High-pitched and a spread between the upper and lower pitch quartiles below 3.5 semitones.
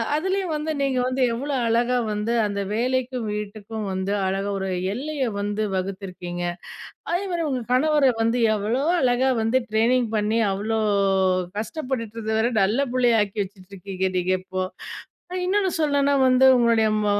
No: high, 225 Hz; average, 4.3 semitones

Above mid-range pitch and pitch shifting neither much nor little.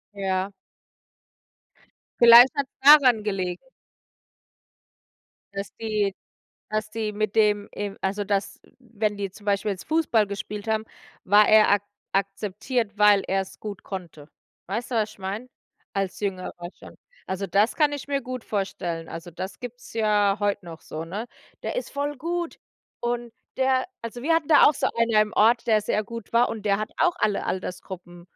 Yes: high, 210 Hz; average, 3.2 semitones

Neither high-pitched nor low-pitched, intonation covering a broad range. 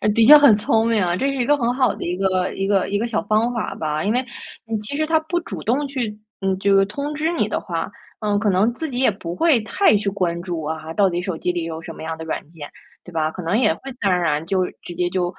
No: high, 200 Hz; wide, 5.7 semitones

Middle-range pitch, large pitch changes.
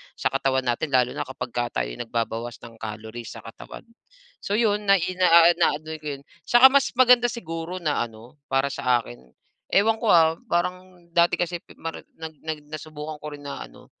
Yes: medium, 155 Hz; wide, 6.3 semitones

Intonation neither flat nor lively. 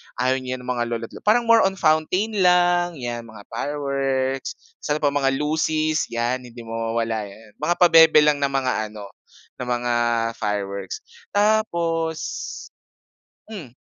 No: wide, 5.8 semitones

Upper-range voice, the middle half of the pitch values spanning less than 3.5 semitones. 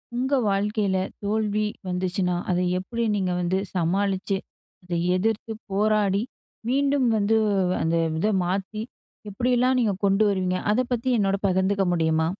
Yes: high, 200 Hz; average, 2.8 semitones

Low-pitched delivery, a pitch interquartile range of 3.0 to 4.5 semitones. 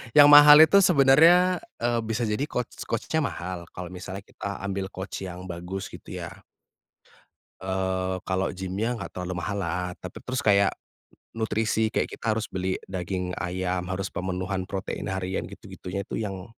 Yes: very low, 95 Hz; average, 3.4 semitones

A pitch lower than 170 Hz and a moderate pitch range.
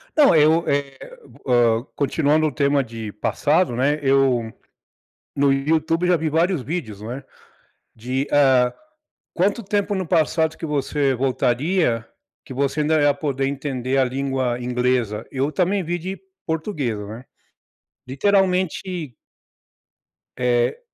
Yes: medium, 140 Hz; average, 4.3 semitones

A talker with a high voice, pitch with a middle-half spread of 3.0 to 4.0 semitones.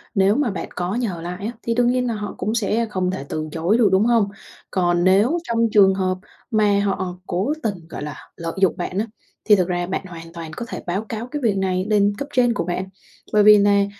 Yes: high, 200 Hz; average, 3.6 semitones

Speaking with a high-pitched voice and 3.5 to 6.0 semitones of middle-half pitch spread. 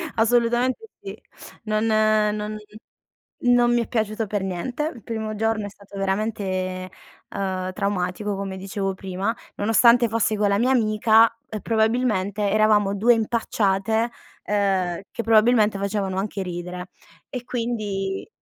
No: high, 210 Hz; narrow, 2.6 semitones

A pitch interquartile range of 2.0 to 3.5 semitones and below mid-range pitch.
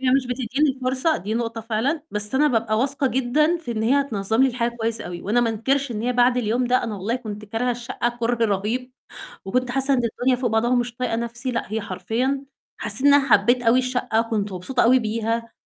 No: narrow, 2.5 semitones; high, 240 Hz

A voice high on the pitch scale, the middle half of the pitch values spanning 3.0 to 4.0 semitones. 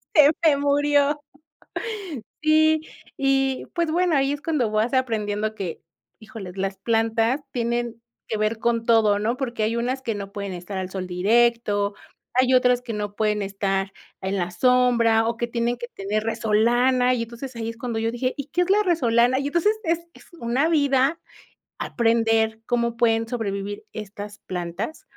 Yes: high, 235 Hz; average, 3.6 semitones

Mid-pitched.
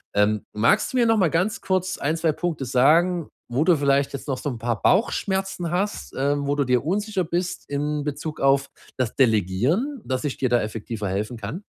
Yes: medium, 145 Hz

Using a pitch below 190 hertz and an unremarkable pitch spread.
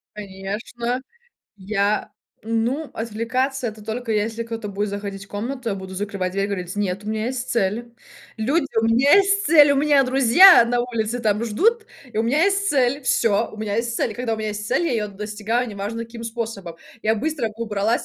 No: high, 225 Hz; average, 3.2 semitones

